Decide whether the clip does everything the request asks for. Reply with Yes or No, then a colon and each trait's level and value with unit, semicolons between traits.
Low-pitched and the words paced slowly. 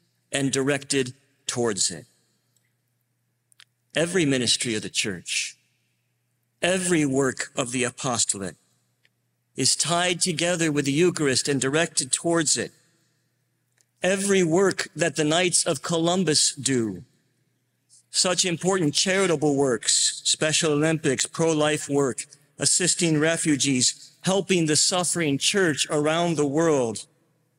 No: medium, 150 Hz; slow, 105 wpm